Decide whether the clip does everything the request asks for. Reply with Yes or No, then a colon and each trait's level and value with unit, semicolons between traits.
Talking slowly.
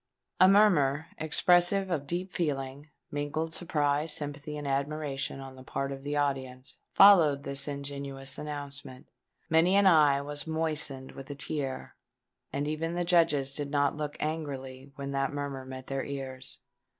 No: average, 145 wpm